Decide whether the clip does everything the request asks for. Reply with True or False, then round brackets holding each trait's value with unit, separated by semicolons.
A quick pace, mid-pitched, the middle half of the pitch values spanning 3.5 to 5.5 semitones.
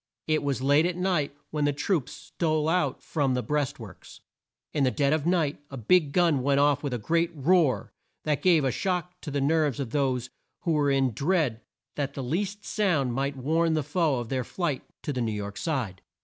True (210 wpm; 145 Hz; 3.8 semitones)